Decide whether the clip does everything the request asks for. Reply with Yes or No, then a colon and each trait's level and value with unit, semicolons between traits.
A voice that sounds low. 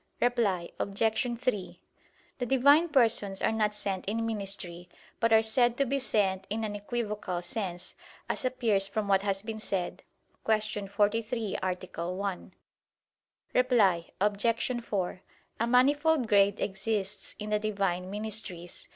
No: high, 210 Hz